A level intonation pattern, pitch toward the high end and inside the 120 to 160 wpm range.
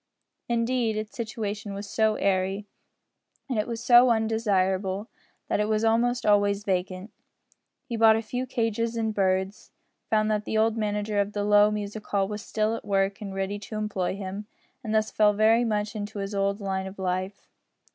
No: narrow, 1.9 semitones; high, 210 Hz; average, 180 wpm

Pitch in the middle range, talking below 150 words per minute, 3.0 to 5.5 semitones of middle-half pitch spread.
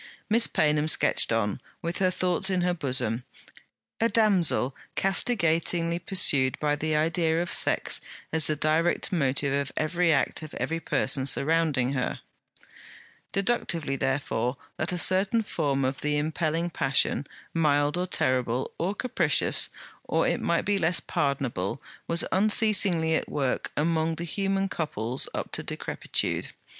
Yes: medium, 160 Hz; average, 140 wpm; average, 4.2 semitones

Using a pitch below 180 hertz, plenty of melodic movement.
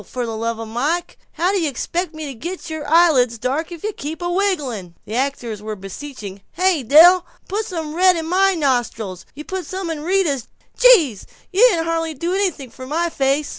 No: very high, 310 Hz; wide, 6.1 semitones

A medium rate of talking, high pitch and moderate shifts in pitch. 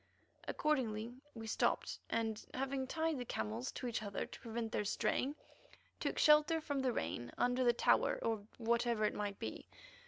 Yes: average, 165 wpm; high, 235 Hz; average, 3.5 semitones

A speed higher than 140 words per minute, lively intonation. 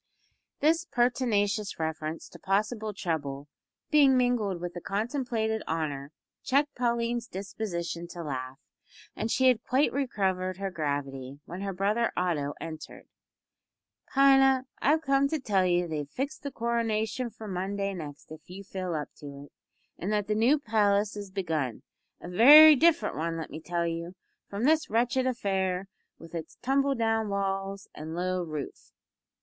Yes: average, 155 wpm; wide, 6.0 semitones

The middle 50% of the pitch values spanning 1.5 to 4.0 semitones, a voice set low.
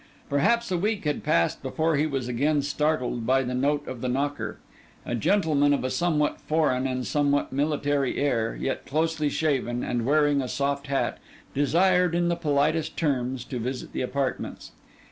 No: average, 3.3 semitones; medium, 145 Hz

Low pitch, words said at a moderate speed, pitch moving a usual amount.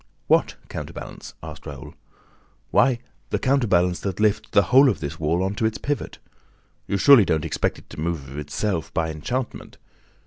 No: very low, 95 Hz; average, 170 wpm; wide, 6.0 semitones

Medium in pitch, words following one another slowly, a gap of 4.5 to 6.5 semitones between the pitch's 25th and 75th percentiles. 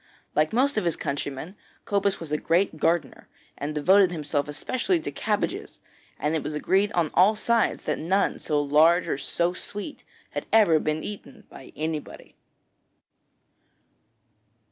No: medium, 170 Hz; average, 145 wpm; average, 5.1 semitones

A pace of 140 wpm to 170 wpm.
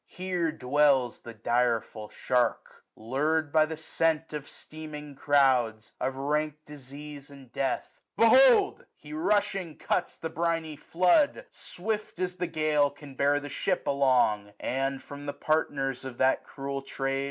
Yes: average, 155 wpm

